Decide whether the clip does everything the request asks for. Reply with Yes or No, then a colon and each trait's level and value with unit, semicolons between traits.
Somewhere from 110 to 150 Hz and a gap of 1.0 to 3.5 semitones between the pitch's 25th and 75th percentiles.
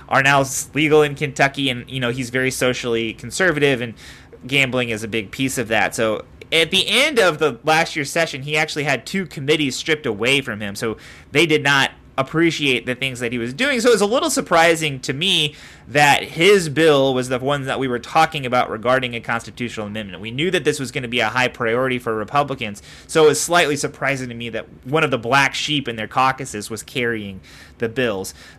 No: low, 135 Hz; average, 4.4 semitones